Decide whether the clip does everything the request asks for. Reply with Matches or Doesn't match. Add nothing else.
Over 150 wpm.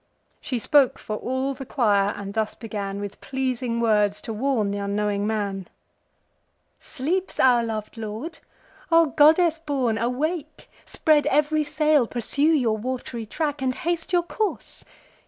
Doesn't match